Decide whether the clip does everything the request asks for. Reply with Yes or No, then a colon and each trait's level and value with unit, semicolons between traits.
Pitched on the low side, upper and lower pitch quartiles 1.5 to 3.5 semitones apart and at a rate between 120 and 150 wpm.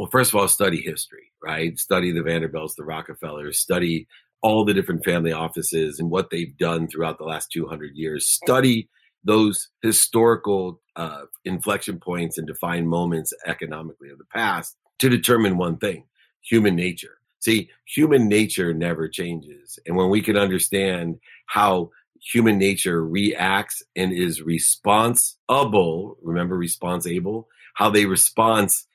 No: very low, 90 Hz; average, 3.9 semitones; average, 140 wpm